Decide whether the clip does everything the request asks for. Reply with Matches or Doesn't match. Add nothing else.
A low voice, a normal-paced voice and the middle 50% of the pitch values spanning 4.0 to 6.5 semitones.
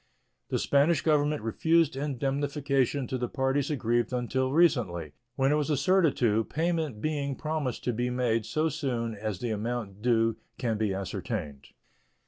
Matches